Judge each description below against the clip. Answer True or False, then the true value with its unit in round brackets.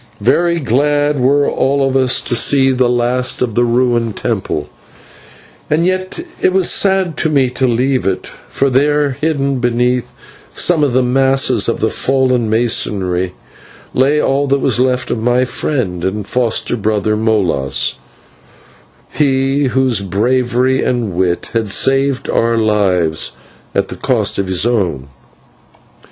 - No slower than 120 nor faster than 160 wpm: True (145 wpm)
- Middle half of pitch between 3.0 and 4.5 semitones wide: True (3.7 semitones)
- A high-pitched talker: False (125 Hz)